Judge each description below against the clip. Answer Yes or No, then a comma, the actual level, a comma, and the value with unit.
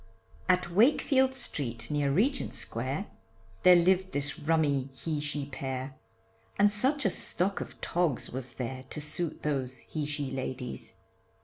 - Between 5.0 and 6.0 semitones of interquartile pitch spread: Yes, average, 5.3 semitones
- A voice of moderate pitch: Yes, medium, 150 Hz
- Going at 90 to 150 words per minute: Yes, average, 140 wpm